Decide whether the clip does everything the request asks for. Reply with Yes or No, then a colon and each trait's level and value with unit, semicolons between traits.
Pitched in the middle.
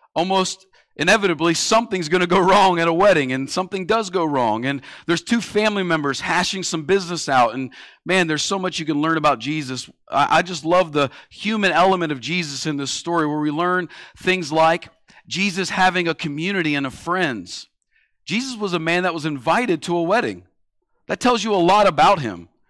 Yes: medium, 170 Hz